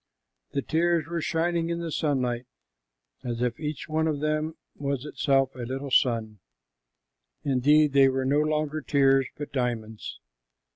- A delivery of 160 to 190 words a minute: No, average, 145 wpm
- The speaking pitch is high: No, medium, 140 Hz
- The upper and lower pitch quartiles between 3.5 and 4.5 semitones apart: No, average, 3.1 semitones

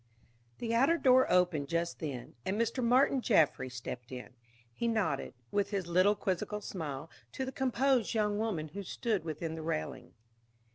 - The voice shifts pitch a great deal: Yes, wide, 6.8 semitones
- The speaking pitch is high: Yes, high, 195 Hz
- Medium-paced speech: Yes, average, 160 wpm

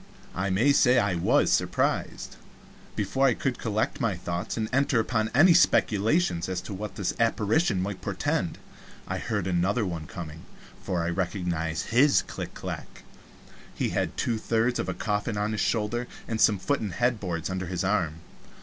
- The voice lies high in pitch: No, low, 105 Hz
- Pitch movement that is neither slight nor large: Yes, average, 4.3 semitones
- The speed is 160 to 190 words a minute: Yes, average, 175 wpm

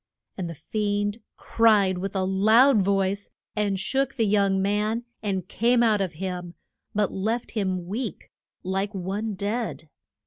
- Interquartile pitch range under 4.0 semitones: Yes, narrow, 2.4 semitones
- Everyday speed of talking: Yes, average, 145 wpm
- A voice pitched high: Yes, high, 200 Hz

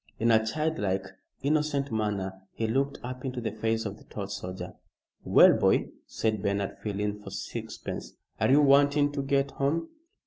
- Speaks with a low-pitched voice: Yes, low, 115 Hz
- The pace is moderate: Yes, average, 170 wpm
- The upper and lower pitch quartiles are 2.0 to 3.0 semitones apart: No, average, 5.2 semitones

